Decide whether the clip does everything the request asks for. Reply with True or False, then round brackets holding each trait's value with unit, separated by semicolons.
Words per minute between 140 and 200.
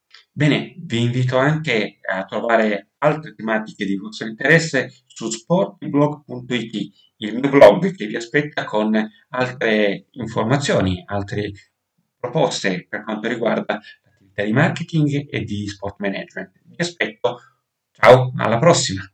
False (120 wpm)